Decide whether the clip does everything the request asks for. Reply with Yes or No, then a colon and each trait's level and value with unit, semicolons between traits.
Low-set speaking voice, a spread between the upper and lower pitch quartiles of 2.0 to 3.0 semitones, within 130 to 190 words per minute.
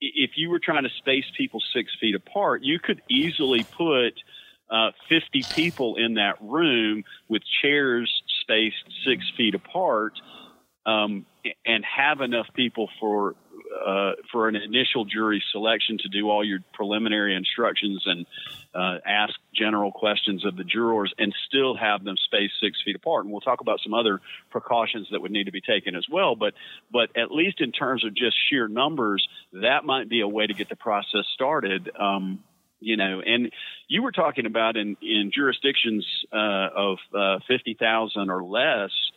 Yes: low, 110 Hz; average, 2.7 semitones; average, 175 wpm